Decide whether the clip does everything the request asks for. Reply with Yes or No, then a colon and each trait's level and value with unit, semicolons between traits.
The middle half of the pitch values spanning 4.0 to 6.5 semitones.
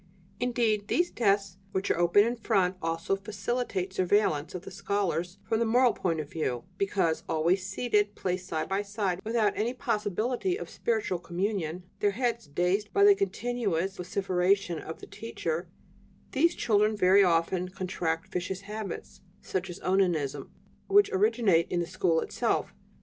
No: average, 3.6 semitones